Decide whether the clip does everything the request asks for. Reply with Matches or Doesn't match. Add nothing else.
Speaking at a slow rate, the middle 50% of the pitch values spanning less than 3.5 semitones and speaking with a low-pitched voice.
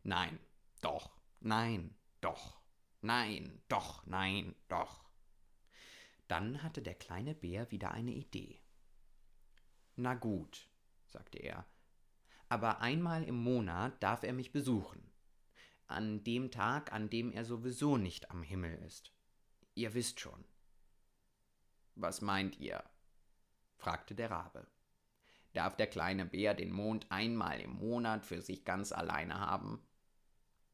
Doesn't match